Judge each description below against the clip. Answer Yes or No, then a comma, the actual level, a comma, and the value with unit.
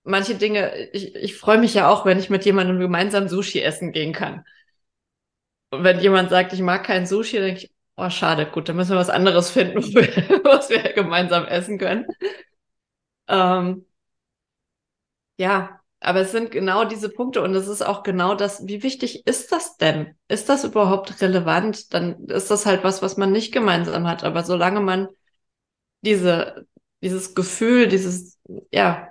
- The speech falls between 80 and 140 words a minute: No, average, 170 wpm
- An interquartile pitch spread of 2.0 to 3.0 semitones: Yes, narrow, 2.4 semitones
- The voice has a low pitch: No, high, 195 Hz